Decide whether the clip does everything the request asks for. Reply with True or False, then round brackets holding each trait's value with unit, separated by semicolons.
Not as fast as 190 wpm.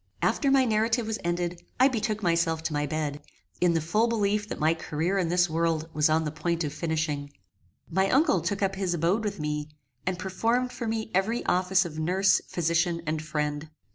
False (200 wpm)